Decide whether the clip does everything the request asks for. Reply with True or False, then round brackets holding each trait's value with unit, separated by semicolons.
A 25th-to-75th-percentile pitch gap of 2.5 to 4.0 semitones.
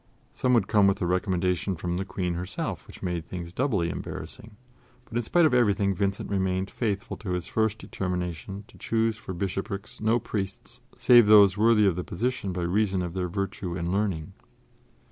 True (3.0 semitones)